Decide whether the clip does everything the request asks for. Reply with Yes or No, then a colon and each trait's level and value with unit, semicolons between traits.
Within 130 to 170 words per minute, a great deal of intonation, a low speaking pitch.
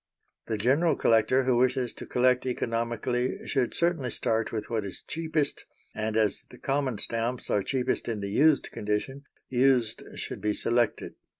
No: average, 160 wpm; average, 2.9 semitones; low, 125 Hz